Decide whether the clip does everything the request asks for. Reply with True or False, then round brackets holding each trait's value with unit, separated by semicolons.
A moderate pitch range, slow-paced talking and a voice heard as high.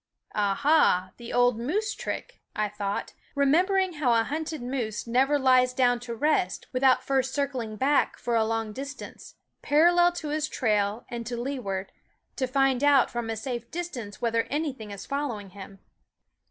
False (4.3 semitones; 165 wpm; 250 Hz)